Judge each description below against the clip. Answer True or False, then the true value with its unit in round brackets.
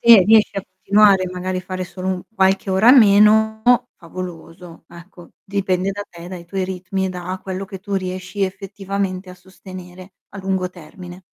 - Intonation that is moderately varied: False (1.4 semitones)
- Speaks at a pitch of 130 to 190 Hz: True (185 Hz)